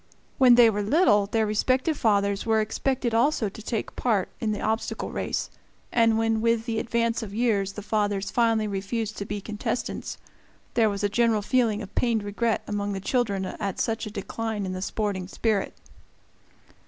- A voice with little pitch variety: Yes, narrow, 2.3 semitones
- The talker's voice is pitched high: Yes, high, 220 Hz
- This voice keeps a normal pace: Yes, average, 180 wpm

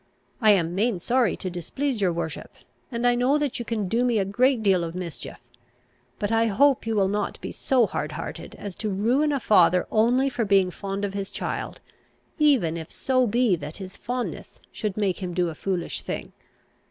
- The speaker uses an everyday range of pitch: Yes, average, 4.8 semitones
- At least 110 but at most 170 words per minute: No, average, 200 wpm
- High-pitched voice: Yes, high, 210 Hz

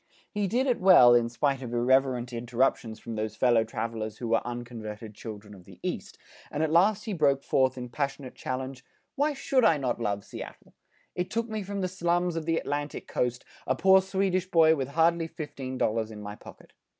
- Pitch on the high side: No, low, 135 Hz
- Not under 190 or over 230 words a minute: Yes, average, 200 wpm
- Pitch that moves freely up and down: Yes, wide, 6.9 semitones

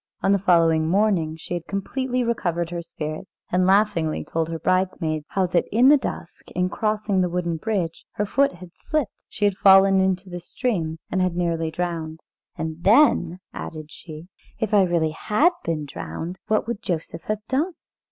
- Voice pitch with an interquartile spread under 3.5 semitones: No, average, 4.0 semitones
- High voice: No, medium, 180 Hz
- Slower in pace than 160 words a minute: No, average, 180 wpm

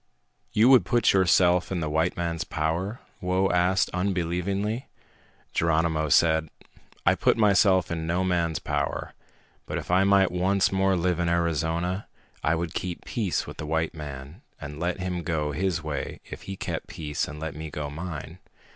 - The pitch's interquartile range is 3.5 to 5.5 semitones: No, average, 2.8 semitones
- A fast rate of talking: No, average, 170 wpm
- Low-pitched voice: Yes, very low, 85 Hz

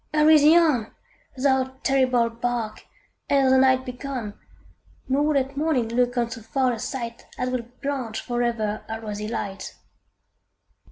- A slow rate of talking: No, average, 155 wpm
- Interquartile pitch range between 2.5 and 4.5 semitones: Yes, average, 2.8 semitones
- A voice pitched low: No, very high, 250 Hz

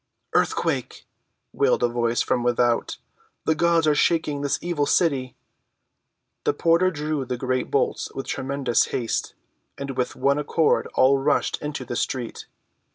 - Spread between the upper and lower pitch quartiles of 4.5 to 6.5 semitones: No, average, 3.6 semitones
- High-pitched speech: No, medium, 140 Hz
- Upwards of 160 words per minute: No, average, 145 wpm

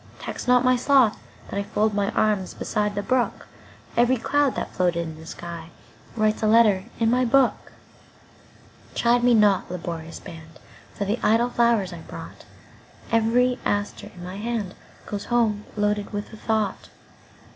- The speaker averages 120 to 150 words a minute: Yes, slow, 135 wpm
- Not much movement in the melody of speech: No, average, 4.1 semitones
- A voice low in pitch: No, high, 210 Hz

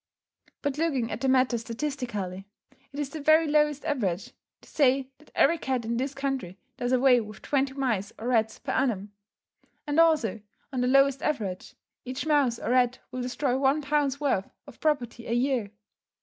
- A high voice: Yes, very high, 260 Hz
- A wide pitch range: No, average, 3.5 semitones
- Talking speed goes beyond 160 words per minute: Yes, average, 180 wpm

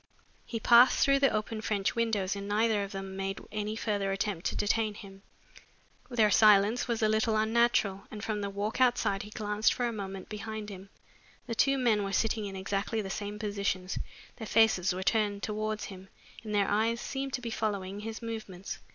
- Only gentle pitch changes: Yes, narrow, 2.1 semitones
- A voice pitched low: No, high, 210 Hz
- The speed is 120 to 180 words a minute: No, average, 195 wpm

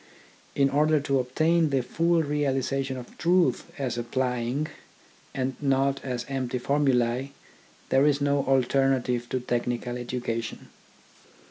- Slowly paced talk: Yes, slow, 120 wpm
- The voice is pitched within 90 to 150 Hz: Yes, low, 135 Hz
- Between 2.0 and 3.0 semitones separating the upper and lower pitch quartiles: Yes, narrow, 2.4 semitones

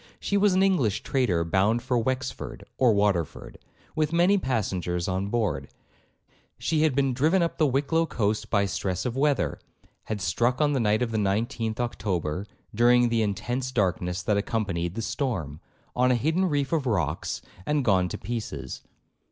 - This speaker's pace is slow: No, average, 170 wpm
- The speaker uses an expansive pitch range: Yes, wide, 5.7 semitones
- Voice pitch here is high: No, low, 115 Hz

